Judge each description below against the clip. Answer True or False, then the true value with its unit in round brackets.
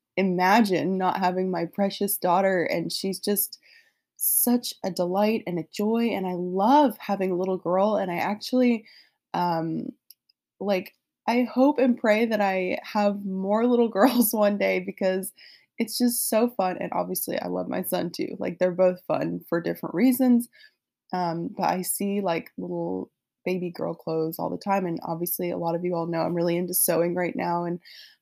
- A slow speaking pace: False (180 wpm)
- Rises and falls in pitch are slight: False (4.0 semitones)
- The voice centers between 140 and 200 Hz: True (190 Hz)